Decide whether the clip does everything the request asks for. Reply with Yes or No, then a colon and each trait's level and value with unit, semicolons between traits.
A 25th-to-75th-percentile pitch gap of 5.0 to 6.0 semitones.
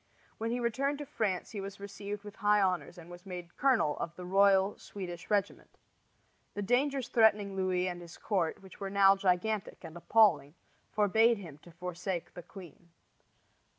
No: average, 2.9 semitones